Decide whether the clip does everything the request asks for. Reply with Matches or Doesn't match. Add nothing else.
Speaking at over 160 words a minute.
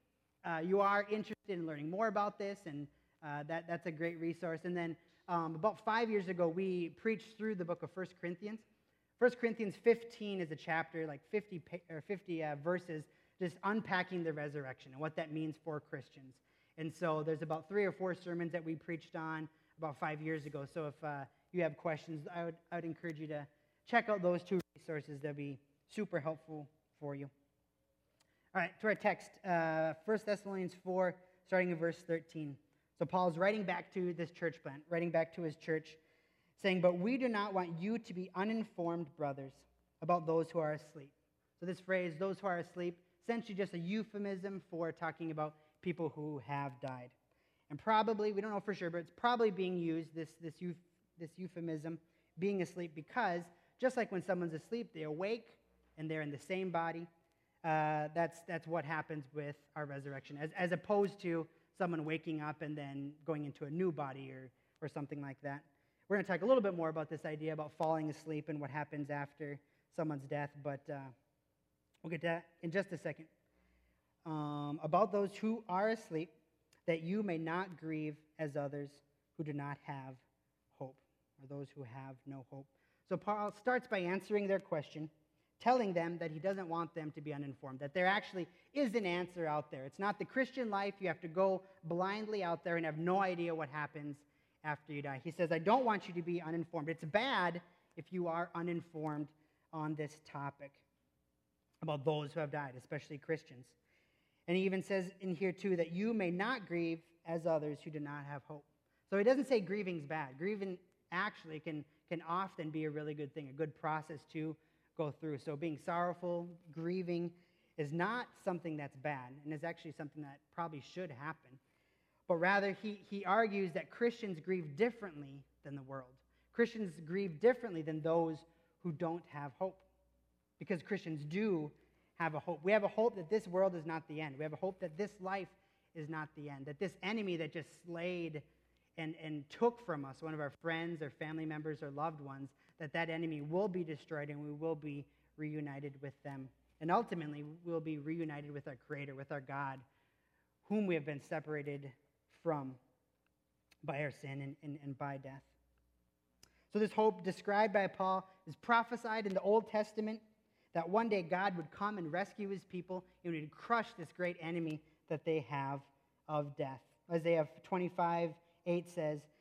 Matches